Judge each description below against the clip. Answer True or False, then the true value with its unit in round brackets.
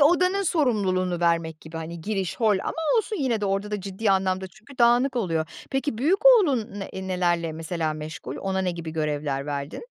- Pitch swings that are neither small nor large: False (6.6 semitones)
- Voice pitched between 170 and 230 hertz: True (190 Hz)